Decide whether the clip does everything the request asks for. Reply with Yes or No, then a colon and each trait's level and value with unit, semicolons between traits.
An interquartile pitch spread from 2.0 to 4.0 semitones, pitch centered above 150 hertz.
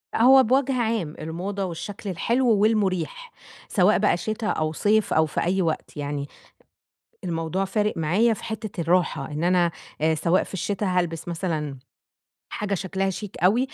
No: average, 4.4 semitones; high, 190 Hz